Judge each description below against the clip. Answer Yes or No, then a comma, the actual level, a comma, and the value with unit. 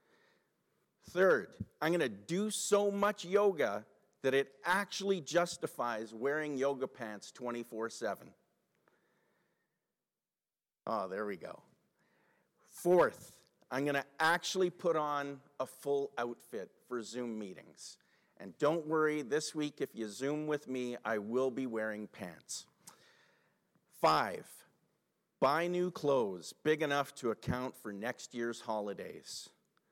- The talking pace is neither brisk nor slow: No, slow, 120 wpm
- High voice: No, medium, 140 Hz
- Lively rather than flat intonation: Yes, wide, 6.3 semitones